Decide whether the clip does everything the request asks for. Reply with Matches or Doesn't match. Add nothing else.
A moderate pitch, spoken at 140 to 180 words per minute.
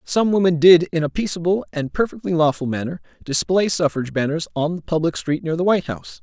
Doesn't match